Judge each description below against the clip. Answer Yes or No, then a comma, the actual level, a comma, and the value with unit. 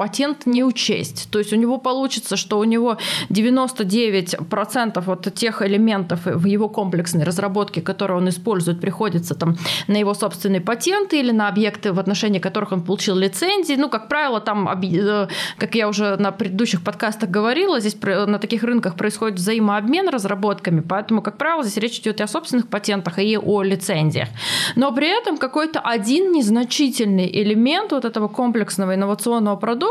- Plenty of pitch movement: No, average, 3.1 semitones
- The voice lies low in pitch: No, high, 210 Hz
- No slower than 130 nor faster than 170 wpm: Yes, fast, 160 wpm